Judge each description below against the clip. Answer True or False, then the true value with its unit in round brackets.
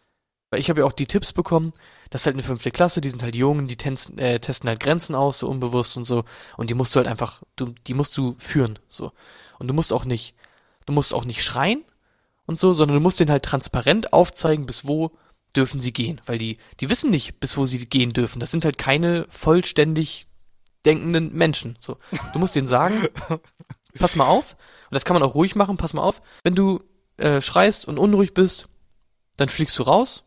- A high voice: False (140 Hz)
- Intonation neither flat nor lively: True (5.0 semitones)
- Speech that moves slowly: False (220 wpm)